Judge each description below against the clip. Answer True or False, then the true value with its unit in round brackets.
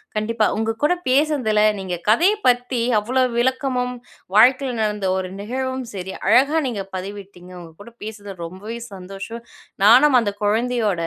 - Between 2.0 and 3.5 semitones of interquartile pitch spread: False (4.2 semitones)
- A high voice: True (225 Hz)